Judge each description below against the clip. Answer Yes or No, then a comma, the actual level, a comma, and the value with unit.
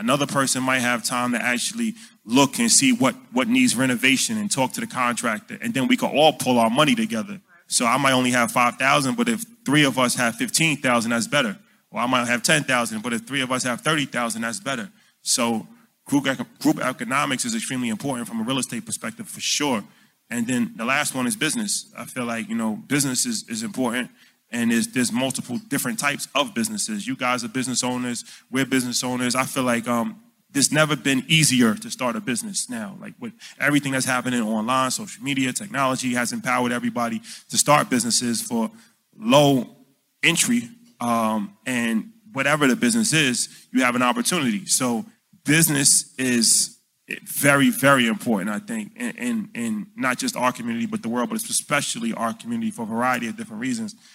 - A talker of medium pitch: Yes, medium, 155 Hz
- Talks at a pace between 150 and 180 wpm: No, average, 190 wpm